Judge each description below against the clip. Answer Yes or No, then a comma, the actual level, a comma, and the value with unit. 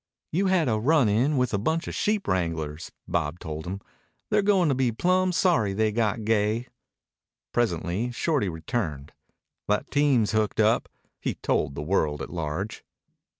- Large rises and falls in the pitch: Yes, wide, 8.2 semitones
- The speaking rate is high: No, average, 160 wpm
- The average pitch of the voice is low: Yes, low, 110 Hz